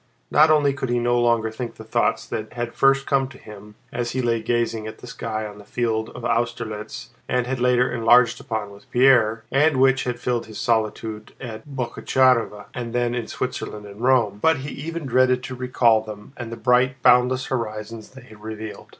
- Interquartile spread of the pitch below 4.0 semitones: Yes, narrow, 2.6 semitones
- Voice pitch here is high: No, low, 120 Hz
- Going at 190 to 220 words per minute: Yes, average, 200 wpm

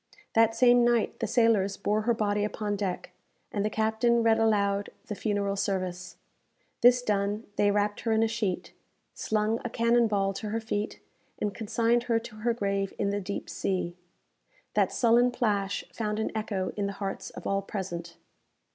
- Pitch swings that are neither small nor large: No, narrow, 2.2 semitones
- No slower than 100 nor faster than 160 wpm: No, average, 175 wpm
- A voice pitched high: Yes, high, 210 Hz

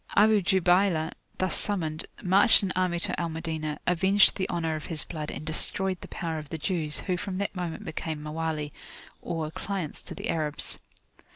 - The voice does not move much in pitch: No, average, 3.1 semitones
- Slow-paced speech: No, average, 180 wpm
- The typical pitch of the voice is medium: Yes, medium, 170 Hz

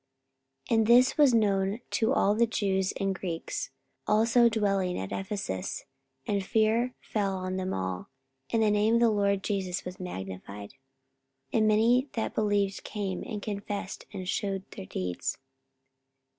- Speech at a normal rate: Yes, average, 155 wpm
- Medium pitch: No, high, 200 Hz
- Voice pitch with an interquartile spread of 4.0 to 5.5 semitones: No, average, 2.8 semitones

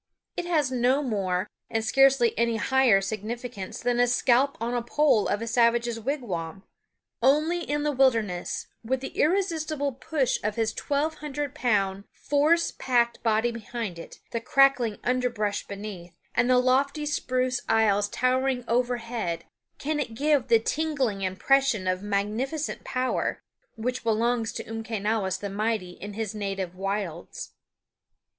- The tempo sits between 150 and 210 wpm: No, average, 140 wpm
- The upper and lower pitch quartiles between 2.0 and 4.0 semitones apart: No, average, 4.4 semitones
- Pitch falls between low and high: No, high, 235 Hz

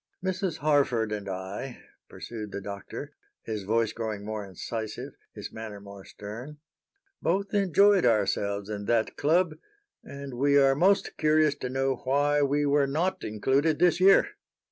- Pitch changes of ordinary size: No, wide, 6.3 semitones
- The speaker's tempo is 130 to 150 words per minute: Yes, average, 145 wpm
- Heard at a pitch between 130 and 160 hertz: Yes, low, 135 Hz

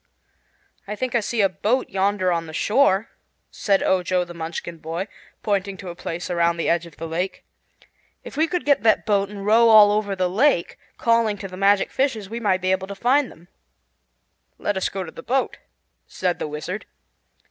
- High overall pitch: Yes, high, 195 Hz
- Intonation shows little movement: No, average, 3.5 semitones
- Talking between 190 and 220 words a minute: Yes, average, 200 wpm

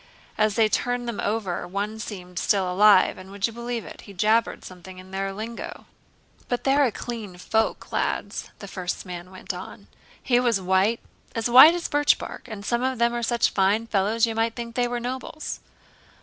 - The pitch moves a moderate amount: Yes, average, 3.7 semitones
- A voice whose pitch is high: Yes, high, 220 Hz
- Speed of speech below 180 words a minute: No, average, 185 wpm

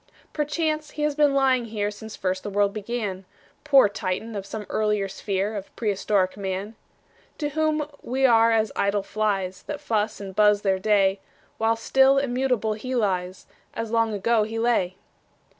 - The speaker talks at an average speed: Yes, average, 165 wpm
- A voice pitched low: No, high, 215 Hz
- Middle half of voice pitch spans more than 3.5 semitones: Yes, average, 4.1 semitones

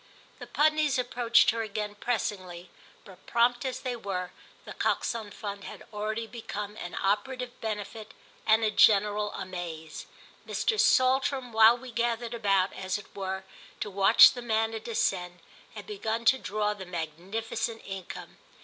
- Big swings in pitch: No, average, 3.3 semitones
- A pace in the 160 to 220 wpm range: No, average, 145 wpm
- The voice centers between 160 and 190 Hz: No, high, 215 Hz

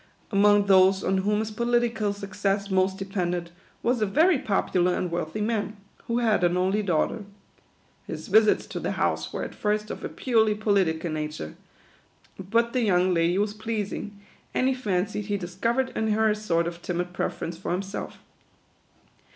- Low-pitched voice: No, high, 200 Hz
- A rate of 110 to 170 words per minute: Yes, average, 165 wpm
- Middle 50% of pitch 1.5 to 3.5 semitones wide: Yes, average, 3.2 semitones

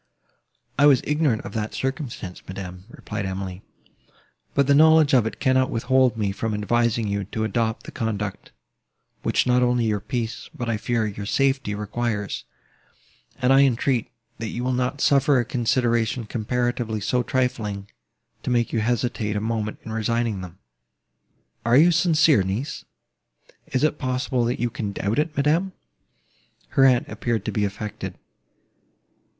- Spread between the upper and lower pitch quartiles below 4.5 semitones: Yes, average, 3.5 semitones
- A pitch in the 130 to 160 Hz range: No, low, 120 Hz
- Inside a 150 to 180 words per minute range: Yes, average, 155 wpm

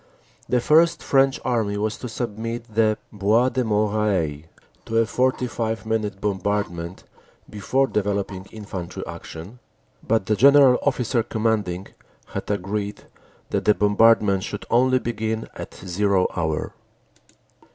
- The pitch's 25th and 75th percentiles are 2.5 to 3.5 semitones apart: Yes, average, 2.9 semitones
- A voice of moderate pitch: No, low, 105 Hz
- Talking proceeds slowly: Yes, slow, 120 wpm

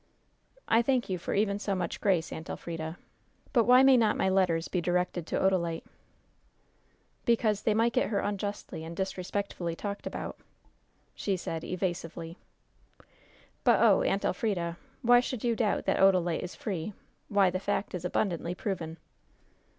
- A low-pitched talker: No, high, 190 Hz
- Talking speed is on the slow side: No, average, 155 wpm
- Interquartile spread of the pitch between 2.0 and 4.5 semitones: Yes, average, 3.6 semitones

